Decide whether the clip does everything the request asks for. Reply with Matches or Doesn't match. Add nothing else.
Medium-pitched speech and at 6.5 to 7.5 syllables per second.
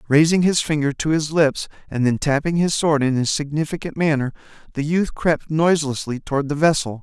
Doesn't match